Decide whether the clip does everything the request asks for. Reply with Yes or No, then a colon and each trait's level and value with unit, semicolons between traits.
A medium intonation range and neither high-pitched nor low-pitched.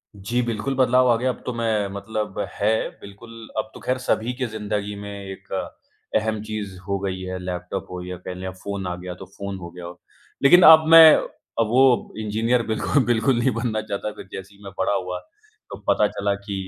No: average, 3.3 semitones; low, 105 Hz